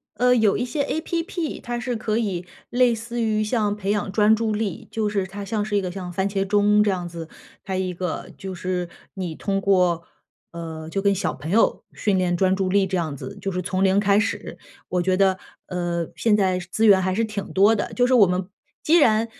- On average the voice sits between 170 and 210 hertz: Yes, high, 200 Hz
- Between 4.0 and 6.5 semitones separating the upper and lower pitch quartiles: No, average, 3.0 semitones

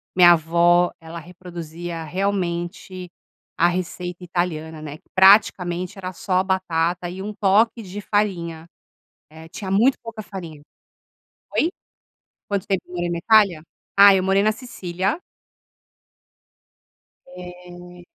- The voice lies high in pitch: No, medium, 180 Hz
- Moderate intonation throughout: No, narrow, 2.2 semitones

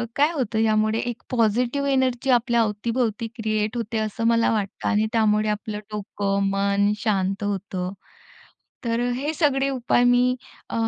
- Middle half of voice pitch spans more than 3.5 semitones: No, average, 2.8 semitones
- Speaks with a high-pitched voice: Yes, high, 225 Hz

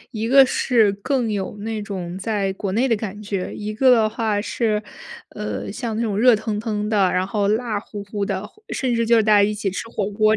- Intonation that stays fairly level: Yes, narrow, 2.0 semitones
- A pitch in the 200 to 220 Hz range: Yes, high, 210 Hz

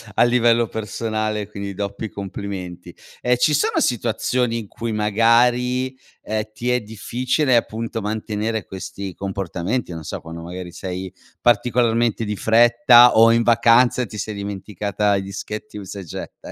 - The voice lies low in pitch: Yes, low, 110 Hz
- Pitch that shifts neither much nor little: Yes, average, 3.1 semitones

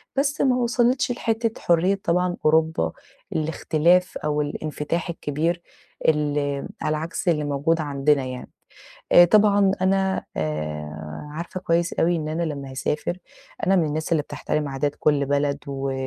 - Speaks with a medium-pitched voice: Yes, medium, 155 Hz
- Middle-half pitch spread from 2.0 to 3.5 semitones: No, average, 3.9 semitones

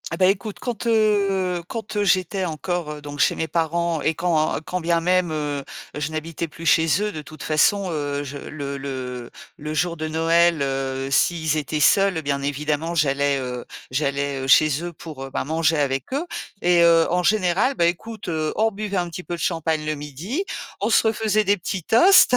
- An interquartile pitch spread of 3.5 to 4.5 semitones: Yes, average, 3.9 semitones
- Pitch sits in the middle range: Yes, medium, 165 Hz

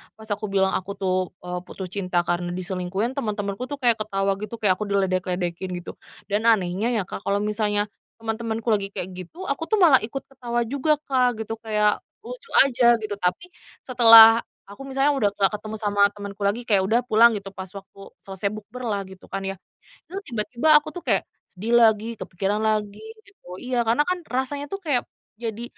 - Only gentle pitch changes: No, average, 3.5 semitones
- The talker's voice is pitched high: Yes, high, 215 Hz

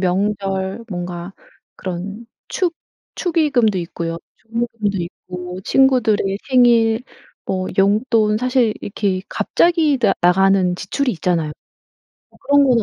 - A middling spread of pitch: Yes, average, 4.7 semitones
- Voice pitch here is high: Yes, high, 205 Hz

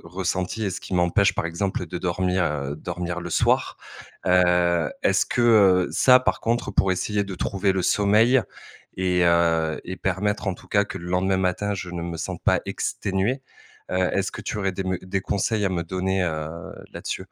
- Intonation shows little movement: Yes, narrow, 2.3 semitones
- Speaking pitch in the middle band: No, very low, 95 Hz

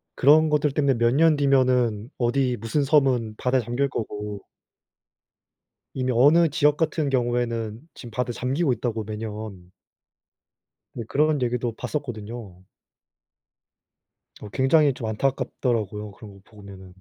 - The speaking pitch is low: Yes, low, 120 Hz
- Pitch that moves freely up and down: No, average, 4.1 semitones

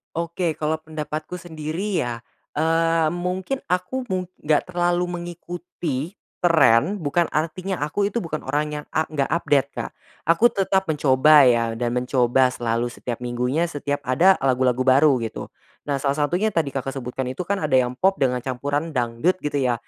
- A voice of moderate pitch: Yes, medium, 150 Hz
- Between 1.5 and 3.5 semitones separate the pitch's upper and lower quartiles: No, average, 5.2 semitones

